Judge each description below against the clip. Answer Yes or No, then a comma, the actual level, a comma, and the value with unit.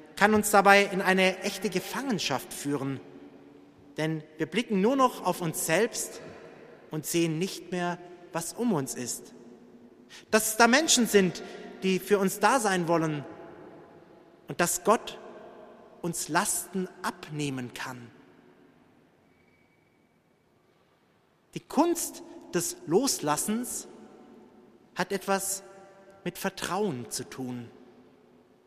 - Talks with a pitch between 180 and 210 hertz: Yes, medium, 185 Hz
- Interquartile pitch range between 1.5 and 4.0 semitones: No, average, 4.9 semitones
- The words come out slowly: Yes, slow, 110 wpm